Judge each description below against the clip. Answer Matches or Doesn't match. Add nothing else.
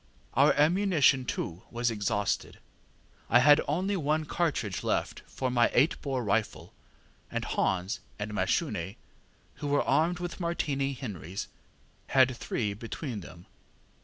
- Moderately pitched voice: Doesn't match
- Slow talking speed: Matches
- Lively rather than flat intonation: Matches